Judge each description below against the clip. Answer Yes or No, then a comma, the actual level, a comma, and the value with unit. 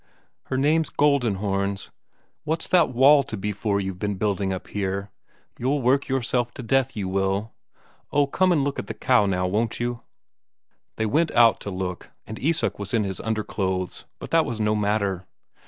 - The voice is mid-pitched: No, low, 110 Hz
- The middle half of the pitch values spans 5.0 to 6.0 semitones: Yes, average, 5.3 semitones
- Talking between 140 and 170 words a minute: No, average, 180 wpm